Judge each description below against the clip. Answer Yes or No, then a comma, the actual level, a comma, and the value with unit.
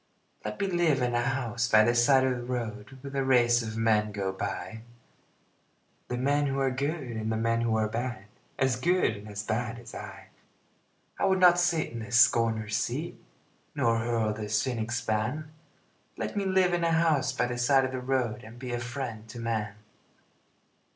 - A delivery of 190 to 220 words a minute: Yes, average, 195 wpm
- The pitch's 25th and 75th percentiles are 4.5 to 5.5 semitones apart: No, average, 3.4 semitones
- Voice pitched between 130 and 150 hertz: No, low, 120 Hz